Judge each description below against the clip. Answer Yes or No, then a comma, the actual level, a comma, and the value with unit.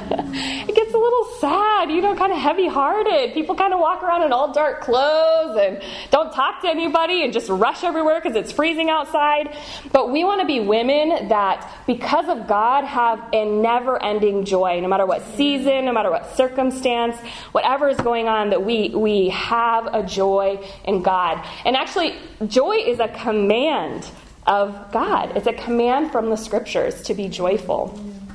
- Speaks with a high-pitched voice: Yes, very high, 260 Hz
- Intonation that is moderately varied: No, wide, 7.0 semitones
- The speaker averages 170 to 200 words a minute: Yes, average, 180 wpm